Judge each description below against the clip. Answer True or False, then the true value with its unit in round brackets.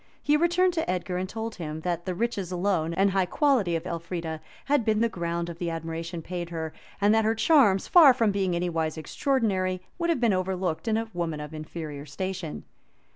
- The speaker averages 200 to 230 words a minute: True (205 wpm)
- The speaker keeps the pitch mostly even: False (4.8 semitones)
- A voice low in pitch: False (185 Hz)